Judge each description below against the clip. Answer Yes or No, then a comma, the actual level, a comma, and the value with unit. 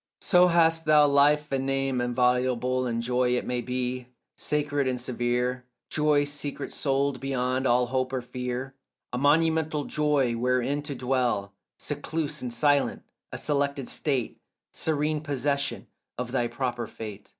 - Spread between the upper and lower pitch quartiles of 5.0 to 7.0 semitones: No, average, 2.7 semitones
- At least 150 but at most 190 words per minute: No, average, 140 wpm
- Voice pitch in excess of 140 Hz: No, low, 135 Hz